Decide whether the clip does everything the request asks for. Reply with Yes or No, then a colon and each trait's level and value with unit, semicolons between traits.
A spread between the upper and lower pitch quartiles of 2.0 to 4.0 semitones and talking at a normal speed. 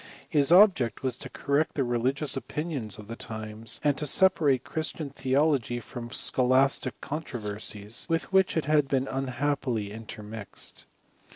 No: average, 4.5 semitones; average, 145 wpm